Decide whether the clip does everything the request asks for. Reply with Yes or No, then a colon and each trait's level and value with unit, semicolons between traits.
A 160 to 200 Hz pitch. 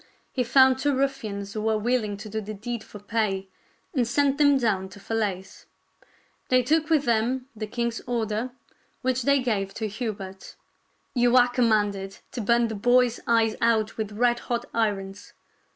No: high, 230 Hz